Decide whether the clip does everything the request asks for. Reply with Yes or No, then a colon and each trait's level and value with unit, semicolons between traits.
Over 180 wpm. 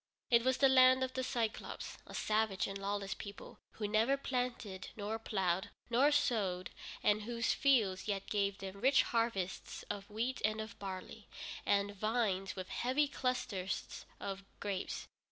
No: average, 155 wpm